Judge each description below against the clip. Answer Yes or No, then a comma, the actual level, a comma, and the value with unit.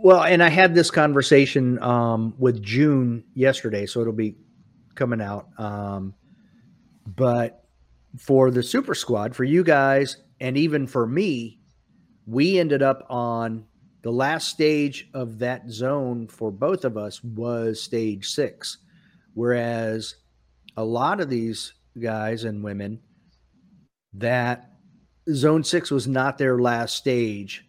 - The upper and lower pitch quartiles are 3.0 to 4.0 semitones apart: Yes, average, 3.5 semitones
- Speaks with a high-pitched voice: No, low, 120 Hz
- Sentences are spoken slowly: Yes, slow, 130 wpm